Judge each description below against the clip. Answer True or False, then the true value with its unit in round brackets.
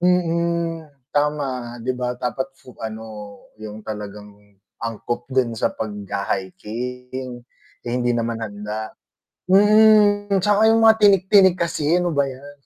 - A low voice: True (130 Hz)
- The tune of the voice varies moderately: False (7.8 semitones)